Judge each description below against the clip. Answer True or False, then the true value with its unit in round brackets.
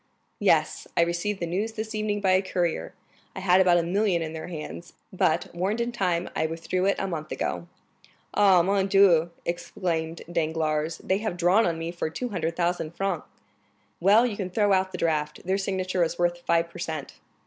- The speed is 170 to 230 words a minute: True (190 wpm)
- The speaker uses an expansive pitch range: False (2.7 semitones)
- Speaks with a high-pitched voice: False (180 Hz)